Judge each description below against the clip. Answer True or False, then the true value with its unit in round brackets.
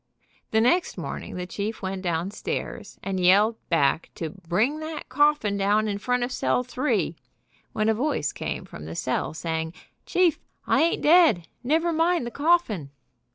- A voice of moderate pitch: False (215 Hz)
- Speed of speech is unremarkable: True (160 wpm)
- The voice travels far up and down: True (8.7 semitones)